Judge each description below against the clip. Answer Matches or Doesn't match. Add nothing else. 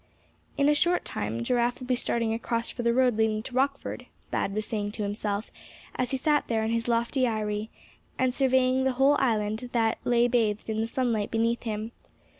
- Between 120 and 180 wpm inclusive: Doesn't match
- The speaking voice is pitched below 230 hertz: Doesn't match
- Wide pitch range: Doesn't match